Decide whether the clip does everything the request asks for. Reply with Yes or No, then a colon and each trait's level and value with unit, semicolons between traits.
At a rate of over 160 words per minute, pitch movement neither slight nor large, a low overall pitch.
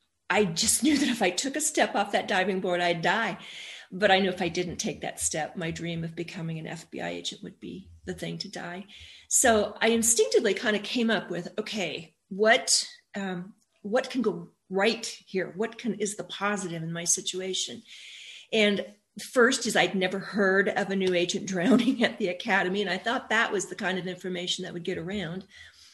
No: fast, 205 wpm; average, 3.7 semitones; high, 195 Hz